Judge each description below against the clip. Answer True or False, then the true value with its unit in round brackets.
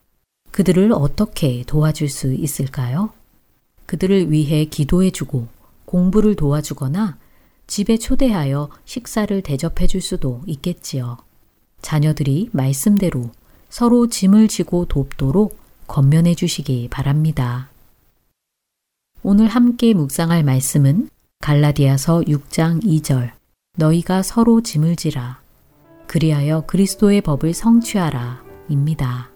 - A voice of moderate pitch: True (155 Hz)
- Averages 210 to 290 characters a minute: True (250 characters per minute)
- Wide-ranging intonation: True (5.7 semitones)